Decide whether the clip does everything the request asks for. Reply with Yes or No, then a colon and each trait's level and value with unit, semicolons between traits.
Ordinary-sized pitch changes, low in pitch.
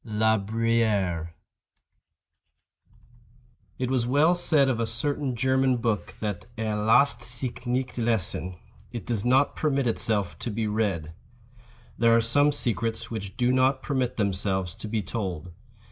Yes: average, 3.6 semitones; low, 115 Hz